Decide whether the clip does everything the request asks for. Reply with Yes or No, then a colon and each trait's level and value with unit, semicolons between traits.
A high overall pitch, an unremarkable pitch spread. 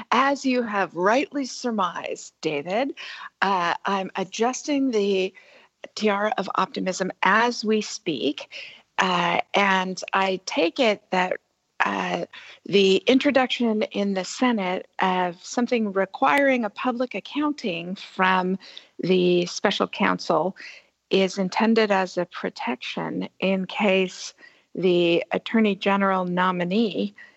Yes: high, 200 Hz; average, 4.6 semitones